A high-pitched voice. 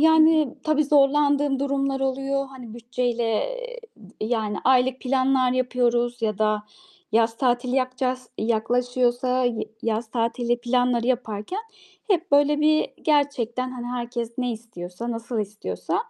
Yes: very high, 250 Hz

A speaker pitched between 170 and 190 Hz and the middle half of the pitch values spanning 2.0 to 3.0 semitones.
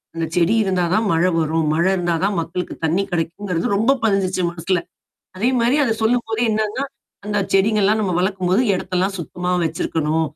No: medium, 185 Hz; average, 3.7 semitones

